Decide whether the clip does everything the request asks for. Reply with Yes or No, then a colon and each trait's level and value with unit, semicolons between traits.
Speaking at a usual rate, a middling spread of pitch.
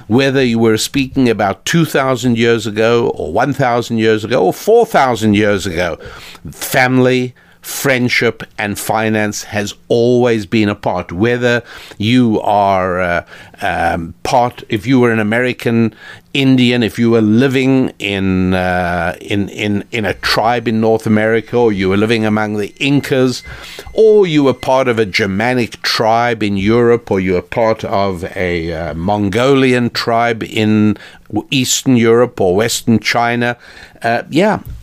Yes: average, 145 wpm; average, 3.2 semitones